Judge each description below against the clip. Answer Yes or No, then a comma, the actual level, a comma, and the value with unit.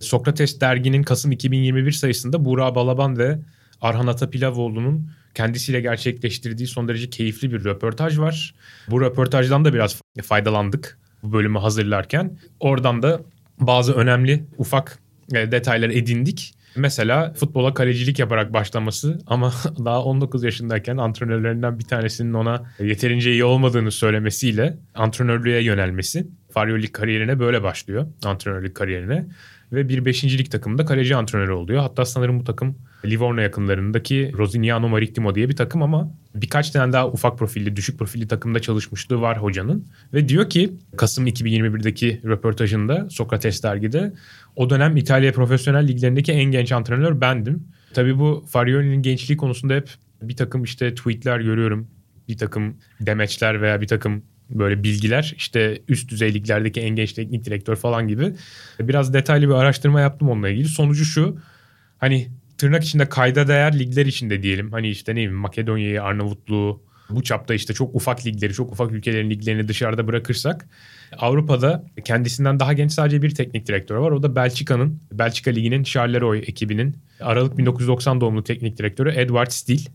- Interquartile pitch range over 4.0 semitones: No, average, 3.5 semitones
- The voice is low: Yes, low, 125 Hz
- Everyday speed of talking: No, fast, 145 wpm